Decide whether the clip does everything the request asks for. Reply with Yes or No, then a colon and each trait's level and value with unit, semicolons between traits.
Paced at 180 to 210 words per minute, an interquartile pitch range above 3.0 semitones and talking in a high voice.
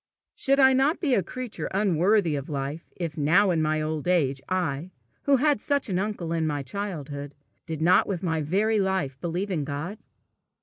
No: average, 185 wpm; average, 5.1 semitones; medium, 175 Hz